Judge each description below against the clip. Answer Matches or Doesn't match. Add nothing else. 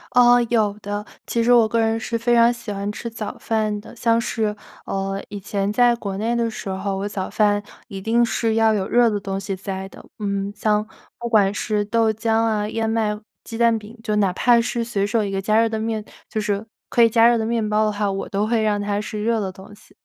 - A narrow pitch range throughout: Matches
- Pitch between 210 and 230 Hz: Matches